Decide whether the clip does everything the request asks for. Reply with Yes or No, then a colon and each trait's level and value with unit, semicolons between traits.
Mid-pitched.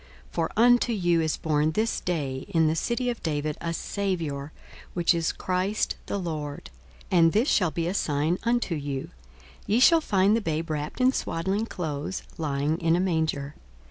Yes: medium, 165 Hz